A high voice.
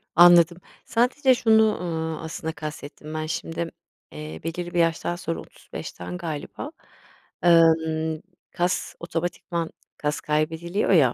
No: medium, 165 Hz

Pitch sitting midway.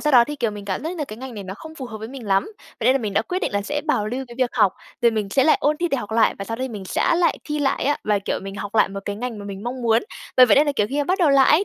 No: high, 240 Hz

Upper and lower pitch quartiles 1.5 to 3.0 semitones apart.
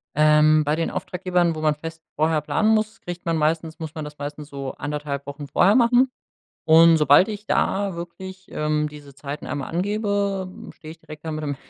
No: average, 3.7 semitones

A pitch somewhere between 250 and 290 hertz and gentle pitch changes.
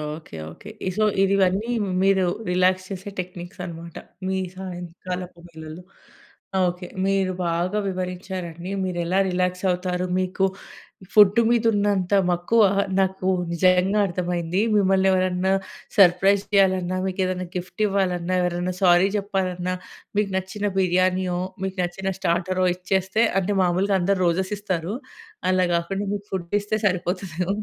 No: medium, 185 Hz; narrow, 1.5 semitones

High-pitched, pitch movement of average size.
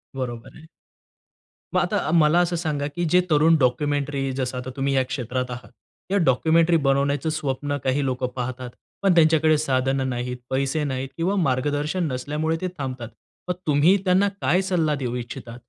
No: medium, 140 Hz; average, 3.6 semitones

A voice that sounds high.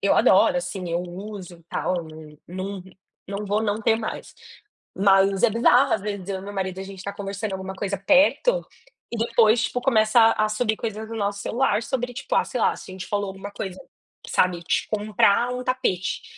Yes: high, 205 Hz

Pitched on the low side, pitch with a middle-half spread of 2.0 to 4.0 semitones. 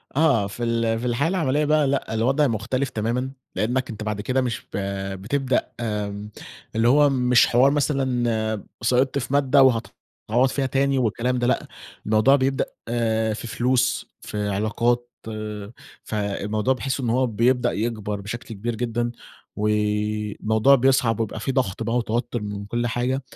Yes: low, 120 Hz; average, 3.3 semitones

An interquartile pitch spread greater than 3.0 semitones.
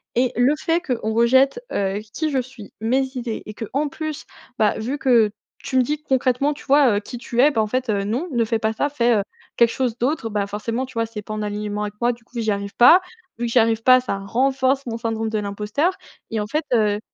Yes: average, 3.6 semitones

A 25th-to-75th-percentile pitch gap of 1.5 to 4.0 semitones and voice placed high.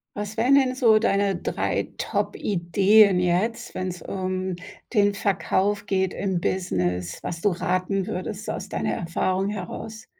Yes: narrow, 2.4 semitones; high, 195 Hz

